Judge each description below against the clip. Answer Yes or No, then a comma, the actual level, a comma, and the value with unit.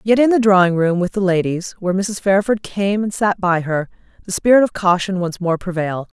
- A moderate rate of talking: No, fast, 225 wpm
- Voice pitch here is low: No, high, 190 Hz